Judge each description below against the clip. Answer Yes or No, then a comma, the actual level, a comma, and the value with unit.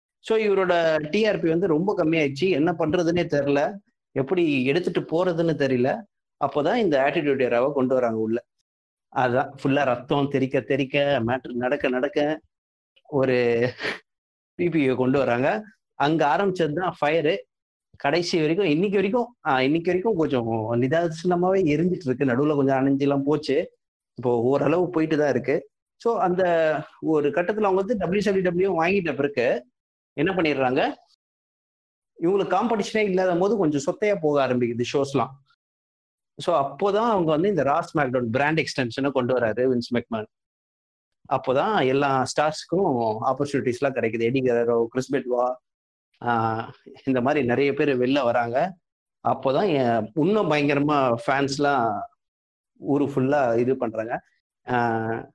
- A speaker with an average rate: Yes, average, 120 wpm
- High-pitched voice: No, medium, 145 Hz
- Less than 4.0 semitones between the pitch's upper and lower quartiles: No, wide, 5.6 semitones